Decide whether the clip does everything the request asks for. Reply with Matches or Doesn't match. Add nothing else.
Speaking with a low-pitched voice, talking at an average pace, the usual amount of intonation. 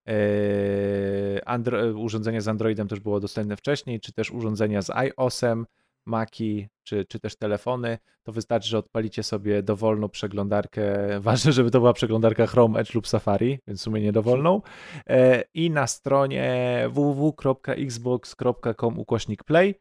Matches